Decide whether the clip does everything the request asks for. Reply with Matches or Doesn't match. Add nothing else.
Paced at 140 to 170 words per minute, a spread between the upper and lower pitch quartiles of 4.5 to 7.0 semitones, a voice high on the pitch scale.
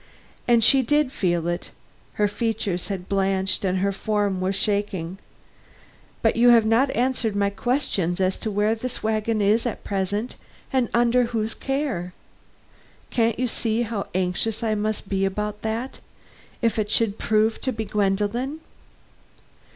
Doesn't match